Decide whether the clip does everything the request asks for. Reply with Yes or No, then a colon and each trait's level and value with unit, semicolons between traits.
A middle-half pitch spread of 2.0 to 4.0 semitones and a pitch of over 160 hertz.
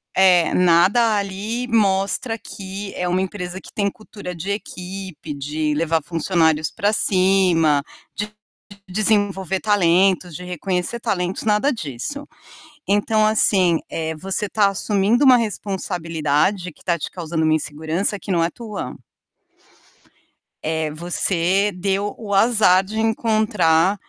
Yes: average, 3.7 semitones; high, 190 Hz